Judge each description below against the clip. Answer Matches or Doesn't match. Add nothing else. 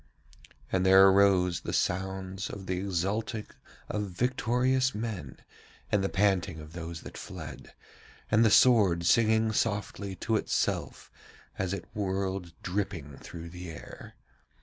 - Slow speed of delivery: Matches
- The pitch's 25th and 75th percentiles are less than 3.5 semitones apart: Matches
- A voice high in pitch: Doesn't match